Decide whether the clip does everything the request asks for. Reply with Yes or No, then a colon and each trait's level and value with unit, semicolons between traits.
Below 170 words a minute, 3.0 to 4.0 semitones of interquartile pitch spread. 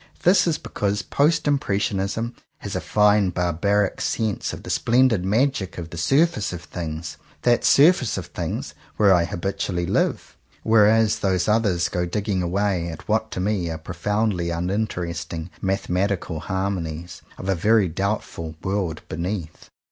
Yes: average, 155 wpm; average, 3.6 semitones